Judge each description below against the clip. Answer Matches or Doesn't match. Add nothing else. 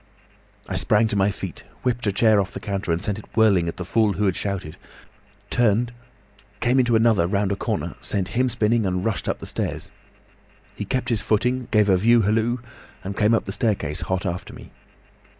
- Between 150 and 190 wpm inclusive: Doesn't match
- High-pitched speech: Doesn't match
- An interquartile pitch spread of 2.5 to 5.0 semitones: Matches